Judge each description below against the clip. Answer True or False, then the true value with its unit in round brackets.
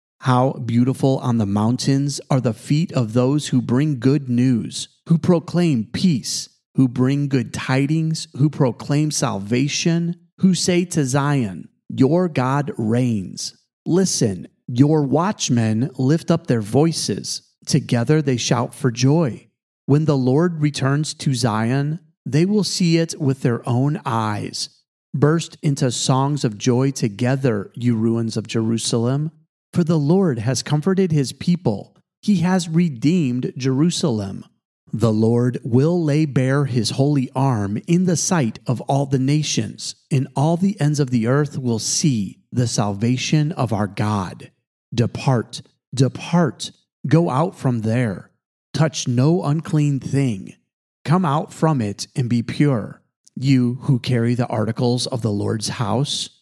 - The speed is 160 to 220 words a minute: False (140 wpm)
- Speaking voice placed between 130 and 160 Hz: True (135 Hz)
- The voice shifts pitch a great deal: False (4.2 semitones)